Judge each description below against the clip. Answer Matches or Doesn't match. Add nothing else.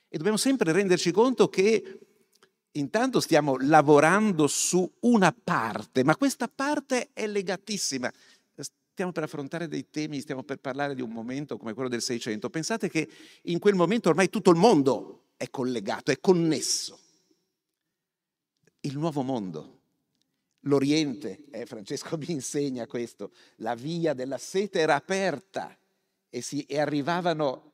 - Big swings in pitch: Matches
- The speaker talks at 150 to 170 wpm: Doesn't match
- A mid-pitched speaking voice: Matches